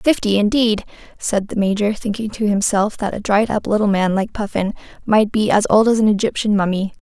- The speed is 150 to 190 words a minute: No, fast, 205 wpm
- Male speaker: No, female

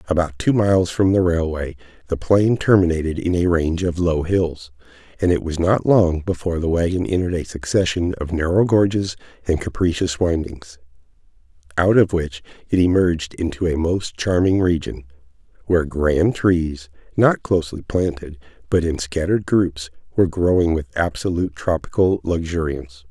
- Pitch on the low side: Yes, very low, 85 Hz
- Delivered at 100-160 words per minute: Yes, average, 150 wpm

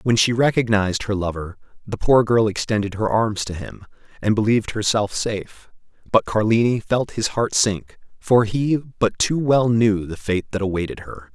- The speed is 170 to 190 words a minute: Yes, average, 180 wpm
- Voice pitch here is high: No, low, 110 Hz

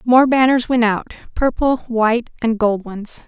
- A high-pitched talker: Yes, high, 235 Hz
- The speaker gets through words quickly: No, average, 145 wpm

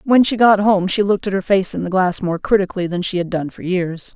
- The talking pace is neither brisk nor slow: No, fast, 290 wpm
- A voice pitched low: No, high, 190 Hz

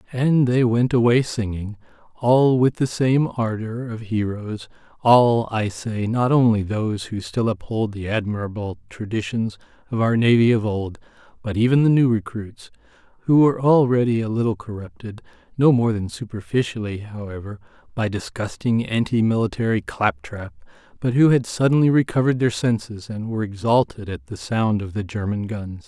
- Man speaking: Yes, male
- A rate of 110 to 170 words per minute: Yes, average, 150 wpm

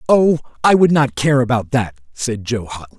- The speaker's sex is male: Yes, male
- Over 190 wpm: Yes, average, 200 wpm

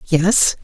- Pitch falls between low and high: Yes, medium, 175 Hz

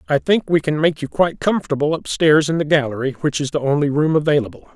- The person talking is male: Yes, male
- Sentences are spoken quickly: Yes, fast, 225 wpm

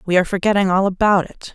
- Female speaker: Yes, female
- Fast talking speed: Yes, fast, 235 wpm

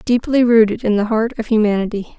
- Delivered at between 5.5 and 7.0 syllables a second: Yes, 5.7 syllables/s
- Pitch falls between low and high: No, high, 225 Hz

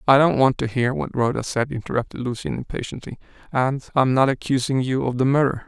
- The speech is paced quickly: Yes, fast, 210 wpm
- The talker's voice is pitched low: Yes, low, 130 Hz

